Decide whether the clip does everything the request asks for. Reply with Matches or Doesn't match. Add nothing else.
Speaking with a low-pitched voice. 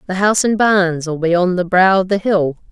Doesn't match